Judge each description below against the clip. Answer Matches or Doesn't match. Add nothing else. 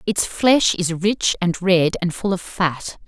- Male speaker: Doesn't match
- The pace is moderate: Matches